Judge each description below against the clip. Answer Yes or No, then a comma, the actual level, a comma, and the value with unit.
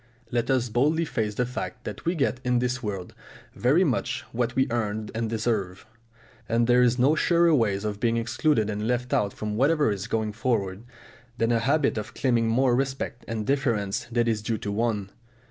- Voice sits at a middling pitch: No, low, 120 Hz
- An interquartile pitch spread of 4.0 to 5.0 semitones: No, average, 3.0 semitones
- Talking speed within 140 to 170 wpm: No, average, 195 wpm